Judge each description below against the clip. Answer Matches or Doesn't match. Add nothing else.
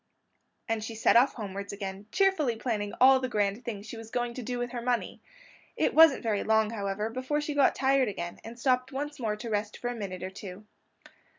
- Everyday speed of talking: Doesn't match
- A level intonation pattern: Doesn't match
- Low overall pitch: Doesn't match